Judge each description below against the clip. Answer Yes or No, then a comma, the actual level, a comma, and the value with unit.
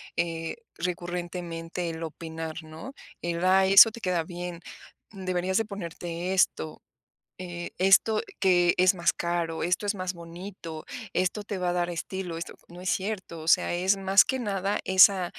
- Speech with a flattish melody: Yes, narrow, 2.1 semitones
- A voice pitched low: No, medium, 180 Hz